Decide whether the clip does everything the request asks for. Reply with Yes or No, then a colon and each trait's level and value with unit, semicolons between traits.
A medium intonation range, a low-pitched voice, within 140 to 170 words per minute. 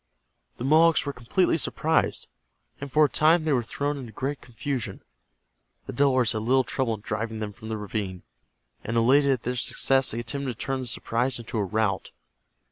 No: average, 4.0 semitones; low, 125 Hz; average, 190 wpm